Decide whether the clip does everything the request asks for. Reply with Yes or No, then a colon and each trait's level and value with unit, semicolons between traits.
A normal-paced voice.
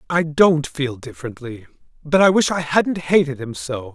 Yes: average, 185 wpm